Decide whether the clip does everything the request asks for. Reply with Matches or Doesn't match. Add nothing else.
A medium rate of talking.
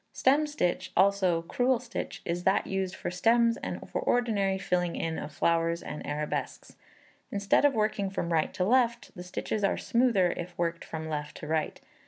Matches